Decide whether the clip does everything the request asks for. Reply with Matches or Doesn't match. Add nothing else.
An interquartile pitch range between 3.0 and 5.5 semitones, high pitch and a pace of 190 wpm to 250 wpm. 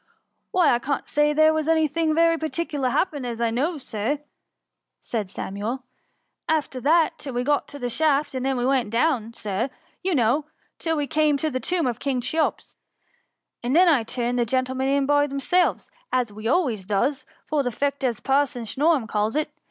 Matches